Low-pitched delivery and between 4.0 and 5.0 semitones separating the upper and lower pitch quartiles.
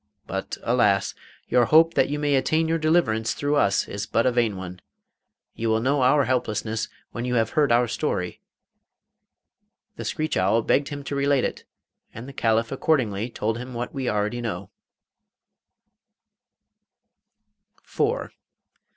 Yes: low, 120 Hz; average, 4.4 semitones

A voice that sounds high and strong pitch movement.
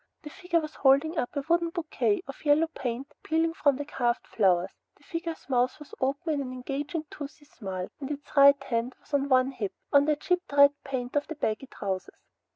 No: very high, 280 Hz; average, 3.5 semitones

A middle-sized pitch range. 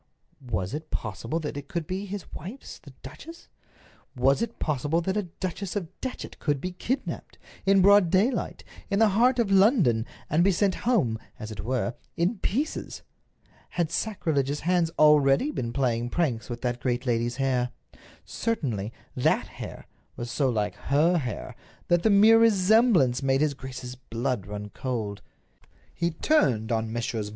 No: wide, 8.1 semitones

